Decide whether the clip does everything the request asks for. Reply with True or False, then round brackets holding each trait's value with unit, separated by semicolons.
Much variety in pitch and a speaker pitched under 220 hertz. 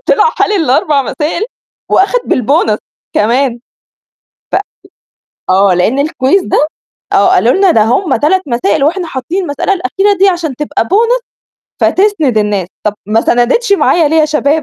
False (7.8 semitones; 300 Hz)